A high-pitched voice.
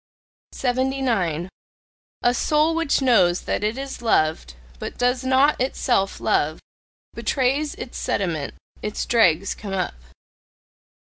Yes: high, 245 Hz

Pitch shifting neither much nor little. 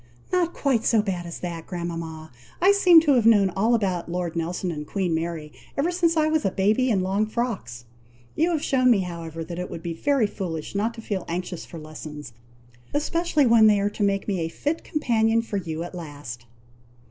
No: wide, 6.1 semitones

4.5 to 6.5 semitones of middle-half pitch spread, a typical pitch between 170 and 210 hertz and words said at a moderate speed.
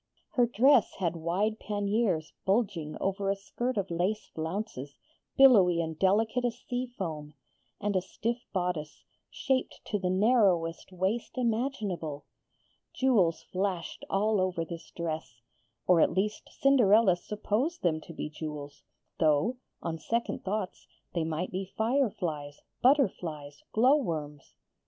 No: average, 5.3 semitones; high, 190 Hz; slow, 130 wpm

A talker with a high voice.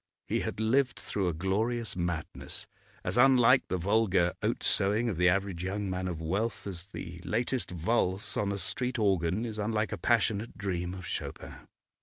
No: low, 100 Hz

